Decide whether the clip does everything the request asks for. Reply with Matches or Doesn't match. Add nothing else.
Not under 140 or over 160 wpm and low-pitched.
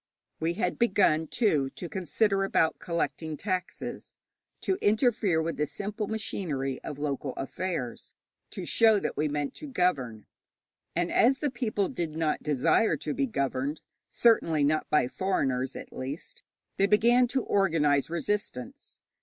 Doesn't match